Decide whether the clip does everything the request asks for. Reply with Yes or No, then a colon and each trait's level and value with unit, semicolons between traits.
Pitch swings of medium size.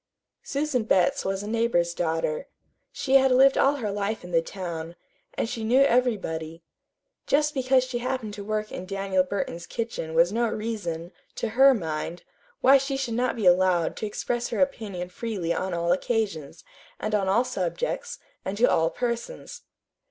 No: wide, 5.9 semitones